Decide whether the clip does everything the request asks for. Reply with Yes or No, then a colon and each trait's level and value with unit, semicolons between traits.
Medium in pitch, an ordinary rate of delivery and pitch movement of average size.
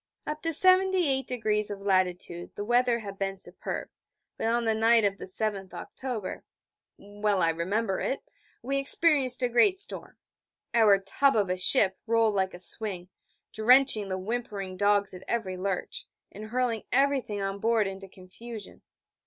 No: high, 215 Hz; average, 155 wpm; average, 4.0 semitones